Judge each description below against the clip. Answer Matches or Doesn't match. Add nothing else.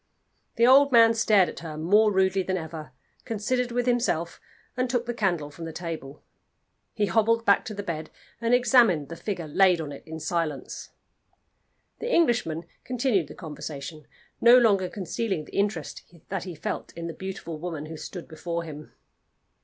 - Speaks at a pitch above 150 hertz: Matches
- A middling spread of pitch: Doesn't match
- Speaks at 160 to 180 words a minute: Matches